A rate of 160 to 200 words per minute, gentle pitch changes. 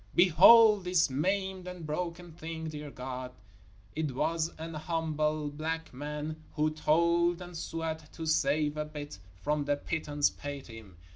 No: average, 150 wpm; narrow, 2.3 semitones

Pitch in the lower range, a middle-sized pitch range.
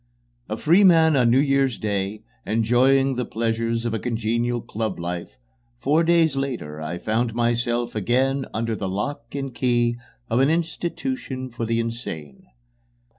Yes: low, 120 Hz; average, 3.4 semitones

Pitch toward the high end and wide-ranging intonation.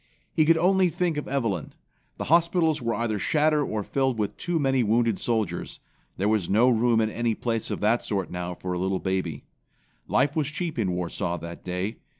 No: low, 115 Hz; wide, 7.5 semitones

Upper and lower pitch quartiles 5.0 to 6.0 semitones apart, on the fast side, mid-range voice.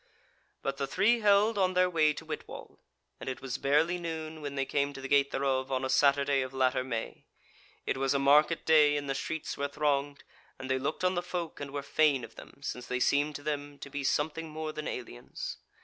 No: narrow, 2.5 semitones; fast, 225 wpm; medium, 145 Hz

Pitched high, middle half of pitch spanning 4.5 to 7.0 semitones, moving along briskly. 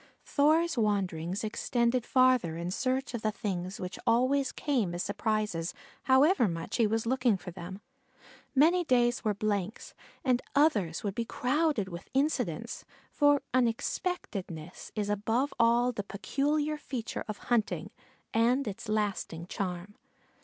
No: high, 225 Hz; average, 4.9 semitones; slow, 135 wpm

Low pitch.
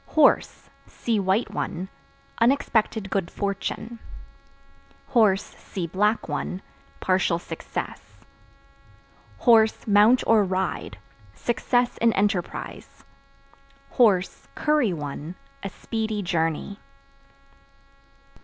No: high, 200 Hz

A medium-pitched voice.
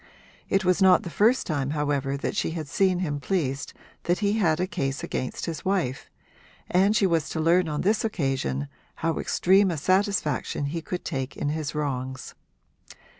Yes: medium, 165 Hz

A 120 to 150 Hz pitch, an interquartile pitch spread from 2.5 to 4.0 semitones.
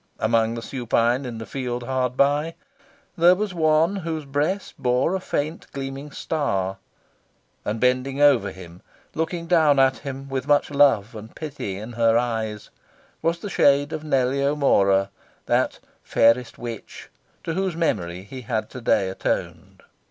No: low, 135 Hz; average, 4.8 semitones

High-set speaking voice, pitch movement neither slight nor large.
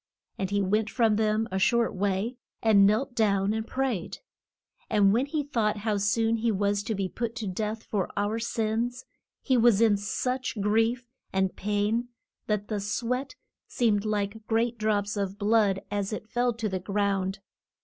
No: high, 215 Hz; narrow, 2.3 semitones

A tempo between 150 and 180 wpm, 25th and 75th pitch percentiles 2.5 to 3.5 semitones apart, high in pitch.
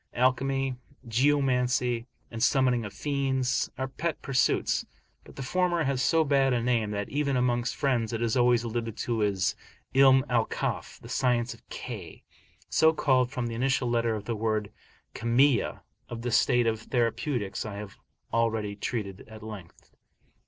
No: average, 160 wpm; average, 2.9 semitones; low, 120 Hz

